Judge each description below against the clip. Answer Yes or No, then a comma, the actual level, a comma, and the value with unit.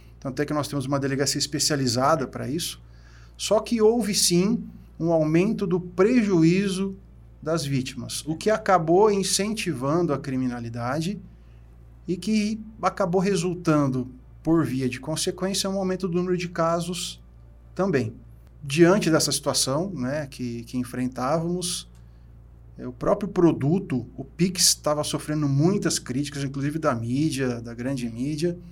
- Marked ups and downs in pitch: Yes, wide, 6.2 semitones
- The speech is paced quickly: No, average, 130 wpm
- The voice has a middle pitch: Yes, medium, 150 Hz